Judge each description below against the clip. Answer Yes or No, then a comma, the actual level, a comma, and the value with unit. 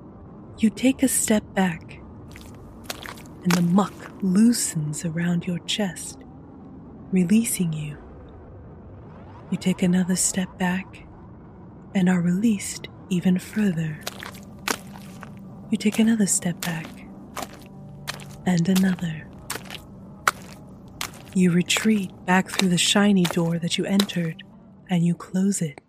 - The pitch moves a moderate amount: No, narrow, 2.3 semitones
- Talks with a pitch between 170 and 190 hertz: Yes, medium, 185 Hz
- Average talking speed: No, slow, 105 wpm